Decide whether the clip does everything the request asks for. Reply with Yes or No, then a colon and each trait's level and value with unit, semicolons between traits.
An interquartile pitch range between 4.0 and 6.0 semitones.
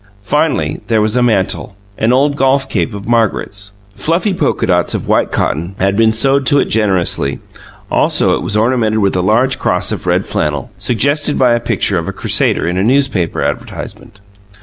Yes: average, 5.2 semitones